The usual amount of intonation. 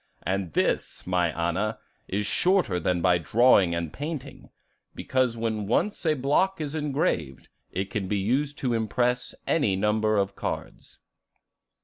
No: wide, 6.6 semitones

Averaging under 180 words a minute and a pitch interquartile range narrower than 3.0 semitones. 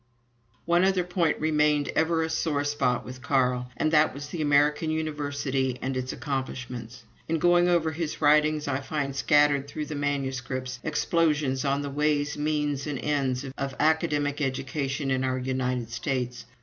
Yes: average, 160 wpm; narrow, 2.6 semitones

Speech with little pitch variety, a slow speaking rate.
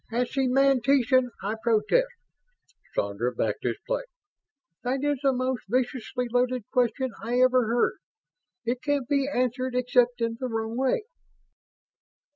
Yes: narrow, 2.0 semitones; slow, 130 wpm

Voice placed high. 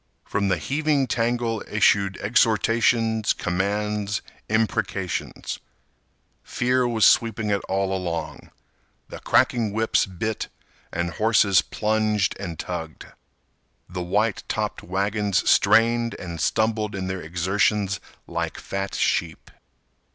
No: low, 105 Hz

